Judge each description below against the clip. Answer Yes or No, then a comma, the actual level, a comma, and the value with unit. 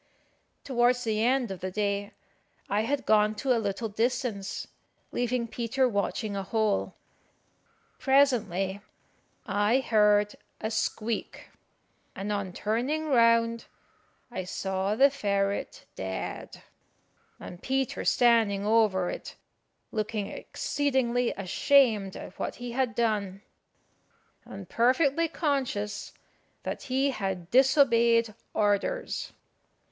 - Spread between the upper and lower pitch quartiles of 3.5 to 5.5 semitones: Yes, average, 3.8 semitones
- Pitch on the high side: Yes, high, 225 Hz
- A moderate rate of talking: No, slow, 105 wpm